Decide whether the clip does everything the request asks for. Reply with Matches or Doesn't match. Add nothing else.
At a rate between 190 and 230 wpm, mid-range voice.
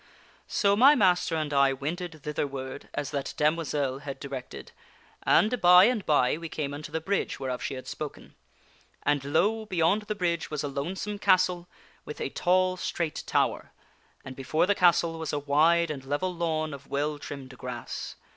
Doesn't match